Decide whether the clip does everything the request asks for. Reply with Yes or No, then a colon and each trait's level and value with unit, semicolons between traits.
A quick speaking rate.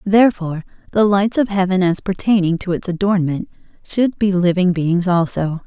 No: average, 160 wpm